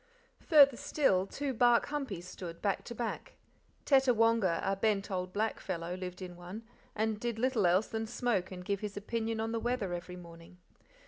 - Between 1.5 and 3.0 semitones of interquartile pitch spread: No, average, 4.2 semitones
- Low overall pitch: No, high, 210 Hz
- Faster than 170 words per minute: Yes, average, 180 wpm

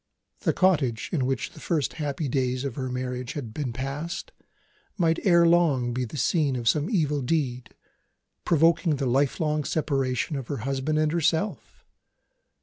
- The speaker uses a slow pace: No, average, 155 wpm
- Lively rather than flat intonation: No, average, 4.0 semitones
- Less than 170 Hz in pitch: Yes, medium, 140 Hz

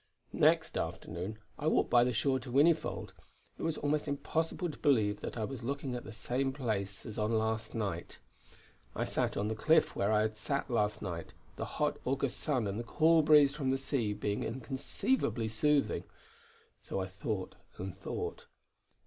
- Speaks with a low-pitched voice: Yes, low, 120 Hz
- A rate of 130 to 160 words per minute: No, average, 180 wpm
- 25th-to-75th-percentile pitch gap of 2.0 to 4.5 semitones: No, average, 4.9 semitones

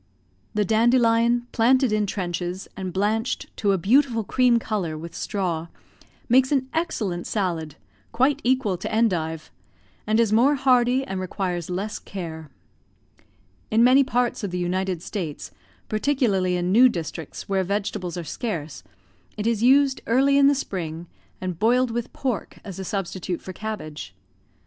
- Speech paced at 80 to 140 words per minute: No, average, 150 wpm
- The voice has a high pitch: Yes, high, 210 Hz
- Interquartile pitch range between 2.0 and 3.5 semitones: No, average, 5.3 semitones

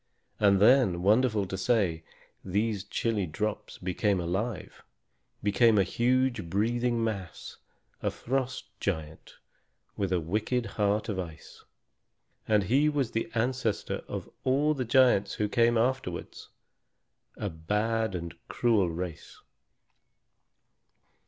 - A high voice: No, low, 105 Hz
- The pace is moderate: No, slow, 115 wpm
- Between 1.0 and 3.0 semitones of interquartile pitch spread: No, average, 4.3 semitones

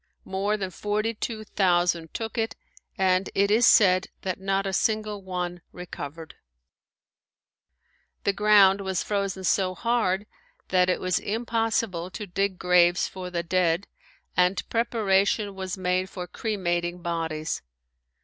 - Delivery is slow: Yes, slow, 130 wpm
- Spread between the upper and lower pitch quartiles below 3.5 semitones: Yes, narrow, 2.5 semitones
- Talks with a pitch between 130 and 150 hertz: No, high, 190 Hz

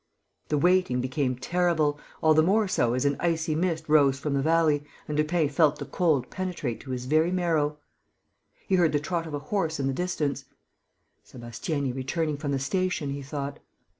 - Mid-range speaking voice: Yes, medium, 150 Hz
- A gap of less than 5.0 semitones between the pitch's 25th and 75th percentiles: Yes, average, 3.2 semitones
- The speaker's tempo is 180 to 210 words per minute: Yes, average, 185 wpm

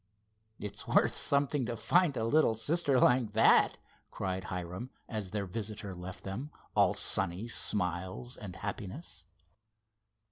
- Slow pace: Yes, slow, 130 wpm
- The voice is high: No, low, 105 Hz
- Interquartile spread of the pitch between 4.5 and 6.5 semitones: Yes, average, 4.8 semitones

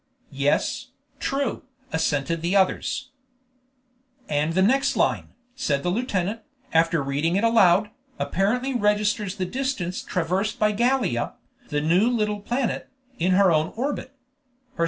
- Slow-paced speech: Yes, slow, 125 wpm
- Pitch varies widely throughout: Yes, wide, 5.9 semitones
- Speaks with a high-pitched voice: Yes, high, 195 Hz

